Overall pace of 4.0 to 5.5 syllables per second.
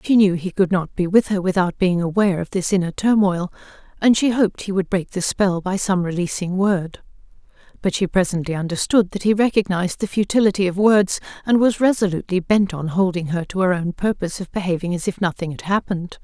No: 5.9 syllables/s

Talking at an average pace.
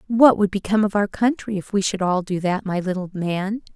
No: fast, 240 wpm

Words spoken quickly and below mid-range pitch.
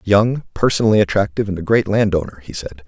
No: average, 190 wpm; very low, 95 Hz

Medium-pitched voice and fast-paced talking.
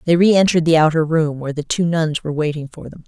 Yes: medium, 160 Hz; fast, 255 wpm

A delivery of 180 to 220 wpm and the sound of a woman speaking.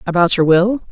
Yes: average, 200 wpm; female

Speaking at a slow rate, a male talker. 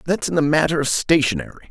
No: fast, 210 wpm; male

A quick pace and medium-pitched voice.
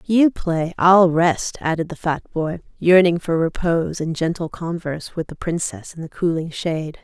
No: average, 180 wpm; medium, 170 Hz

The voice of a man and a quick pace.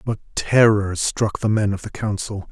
No: male; average, 190 wpm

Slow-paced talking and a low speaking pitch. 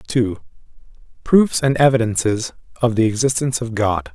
Yes: slow, 130 wpm; low, 120 Hz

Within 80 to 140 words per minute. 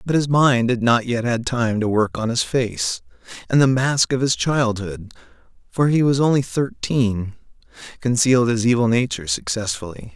No: average, 160 wpm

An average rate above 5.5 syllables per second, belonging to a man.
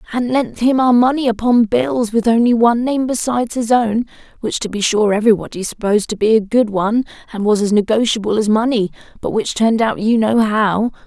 No: 5.8 syllables/s; female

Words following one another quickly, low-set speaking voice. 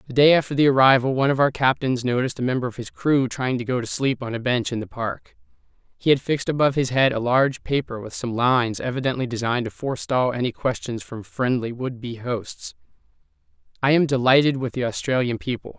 Yes: fast, 215 wpm; low, 125 Hz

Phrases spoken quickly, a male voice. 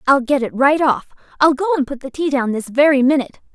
No: fast, 235 wpm; female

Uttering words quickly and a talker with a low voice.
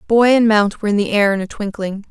No: fast, 285 wpm; high, 210 Hz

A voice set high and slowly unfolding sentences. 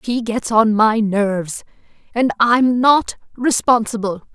Yes: high, 225 Hz; slow, 125 wpm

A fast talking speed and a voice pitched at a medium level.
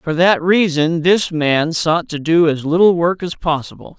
No: average, 195 wpm; medium, 165 Hz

